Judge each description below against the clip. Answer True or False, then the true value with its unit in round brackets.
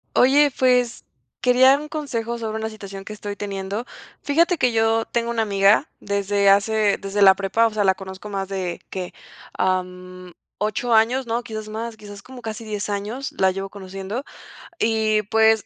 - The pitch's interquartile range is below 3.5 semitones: True (3.0 semitones)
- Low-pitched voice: False (215 Hz)